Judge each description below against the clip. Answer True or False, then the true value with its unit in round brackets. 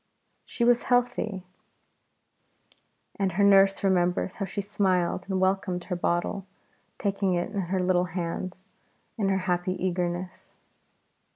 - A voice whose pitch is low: False (190 Hz)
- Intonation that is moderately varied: False (1.7 semitones)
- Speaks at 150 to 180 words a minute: False (135 wpm)